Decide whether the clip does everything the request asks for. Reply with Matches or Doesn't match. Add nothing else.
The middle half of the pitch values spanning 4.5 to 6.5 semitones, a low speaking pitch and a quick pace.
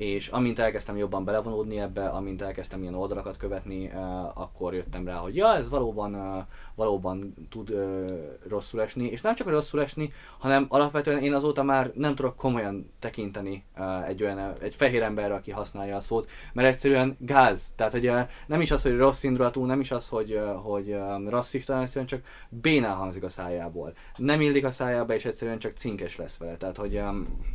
Matches